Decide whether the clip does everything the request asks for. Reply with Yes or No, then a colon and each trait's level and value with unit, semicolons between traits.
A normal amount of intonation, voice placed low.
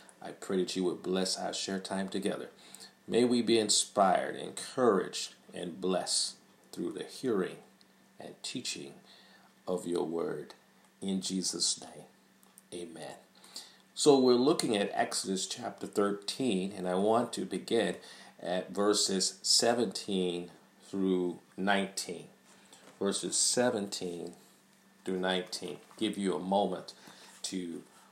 No: narrow, 1.9 semitones; very low, 95 Hz